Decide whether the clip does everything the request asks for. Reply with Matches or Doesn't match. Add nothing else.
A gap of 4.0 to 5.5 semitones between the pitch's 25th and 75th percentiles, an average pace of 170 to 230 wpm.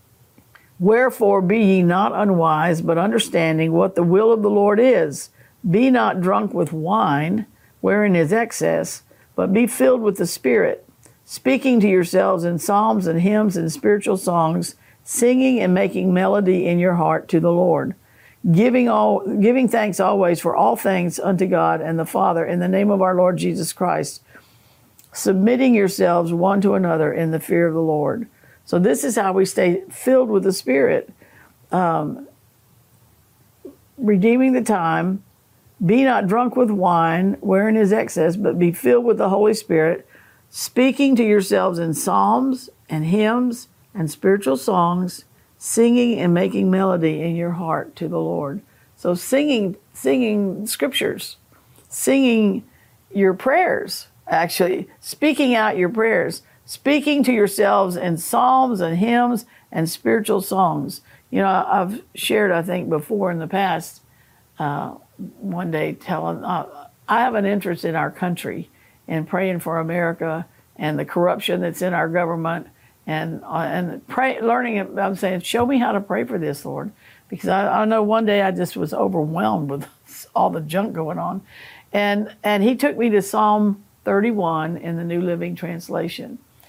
Doesn't match